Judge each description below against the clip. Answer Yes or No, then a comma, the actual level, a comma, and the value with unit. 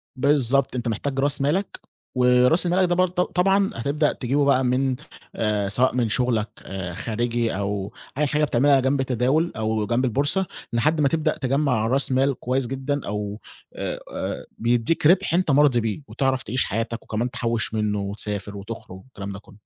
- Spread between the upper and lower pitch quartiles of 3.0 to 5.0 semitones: Yes, average, 4.2 semitones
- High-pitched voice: No, low, 125 Hz